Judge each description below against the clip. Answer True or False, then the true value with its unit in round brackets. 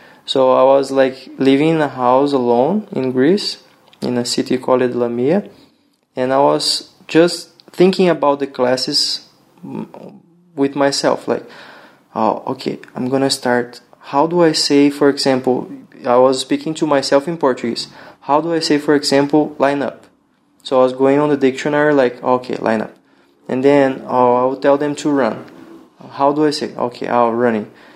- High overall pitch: False (140 Hz)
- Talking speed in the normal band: False (175 wpm)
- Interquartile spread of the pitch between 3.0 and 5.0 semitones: False (2.6 semitones)